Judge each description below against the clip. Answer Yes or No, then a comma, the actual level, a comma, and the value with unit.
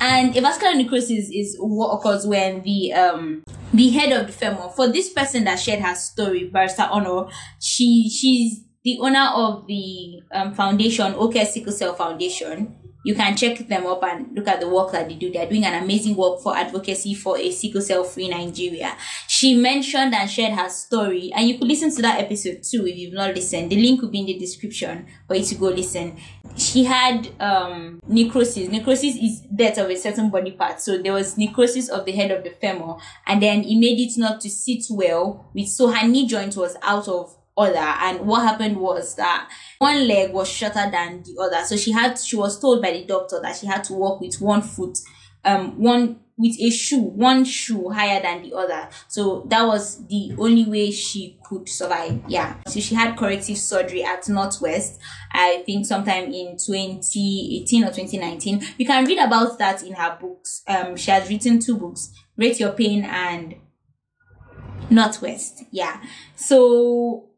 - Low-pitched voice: No, high, 205 Hz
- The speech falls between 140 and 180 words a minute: No, average, 195 wpm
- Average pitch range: Yes, average, 3.8 semitones